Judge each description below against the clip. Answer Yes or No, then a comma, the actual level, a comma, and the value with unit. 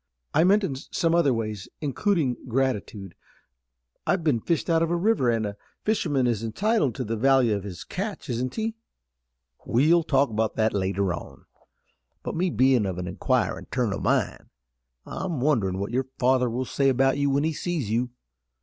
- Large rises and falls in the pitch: Yes, wide, 6.3 semitones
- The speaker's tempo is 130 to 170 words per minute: No, average, 180 wpm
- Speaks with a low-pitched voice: Yes, low, 130 Hz